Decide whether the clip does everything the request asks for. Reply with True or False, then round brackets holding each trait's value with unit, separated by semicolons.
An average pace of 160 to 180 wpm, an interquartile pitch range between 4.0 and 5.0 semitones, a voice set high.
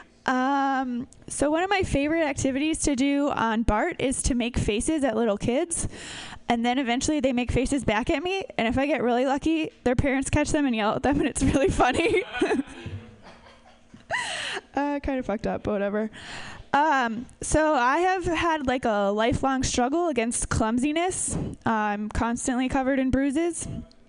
True (170 wpm; 4.4 semitones; 265 Hz)